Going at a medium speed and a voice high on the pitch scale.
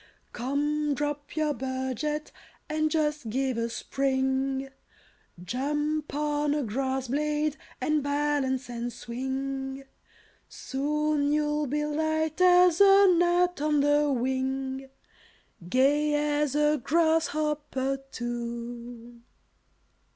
No: slow, 100 wpm; very high, 290 Hz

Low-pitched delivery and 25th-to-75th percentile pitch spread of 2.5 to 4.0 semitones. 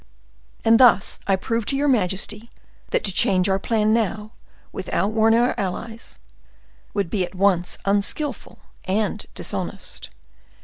No: high, 210 Hz; average, 2.9 semitones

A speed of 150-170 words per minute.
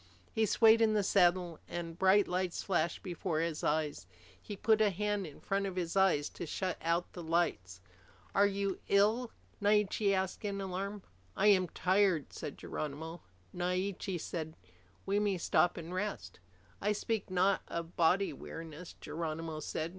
Yes: average, 160 wpm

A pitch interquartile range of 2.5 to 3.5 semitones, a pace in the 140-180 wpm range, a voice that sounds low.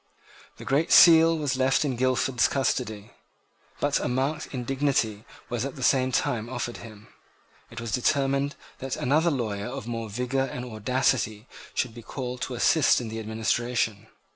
Yes: average, 2.9 semitones; average, 165 wpm; low, 125 Hz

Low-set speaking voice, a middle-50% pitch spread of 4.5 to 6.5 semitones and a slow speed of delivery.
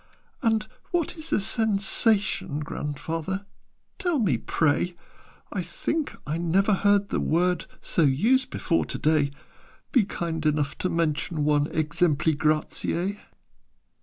No: medium, 170 Hz; average, 5.1 semitones; slow, 125 wpm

